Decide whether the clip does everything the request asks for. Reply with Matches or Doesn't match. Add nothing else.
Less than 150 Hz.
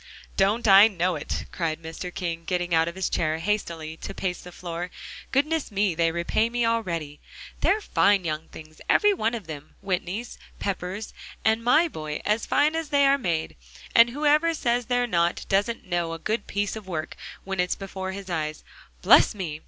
Doesn't match